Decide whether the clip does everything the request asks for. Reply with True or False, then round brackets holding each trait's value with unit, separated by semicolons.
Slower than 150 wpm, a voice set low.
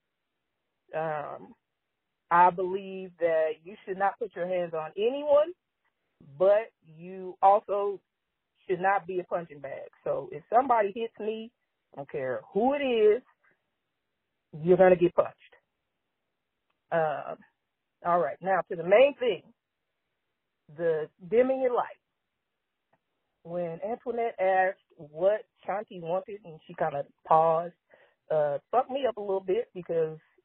False (135 wpm; 190 Hz)